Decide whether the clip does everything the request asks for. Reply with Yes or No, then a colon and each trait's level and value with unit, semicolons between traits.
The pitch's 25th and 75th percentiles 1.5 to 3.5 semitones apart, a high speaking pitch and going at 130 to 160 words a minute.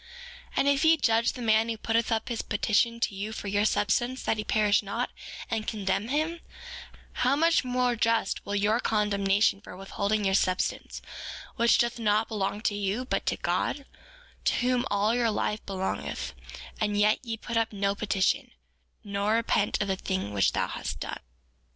No: average, 2.7 semitones; high, 215 Hz; average, 185 wpm